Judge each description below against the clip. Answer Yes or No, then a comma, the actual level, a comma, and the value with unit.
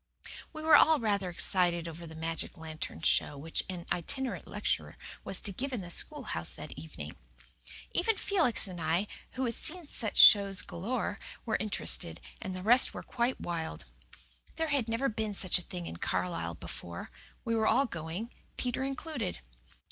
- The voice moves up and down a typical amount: No, wide, 7.4 semitones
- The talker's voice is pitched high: Yes, high, 200 Hz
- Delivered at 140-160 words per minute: No, average, 170 wpm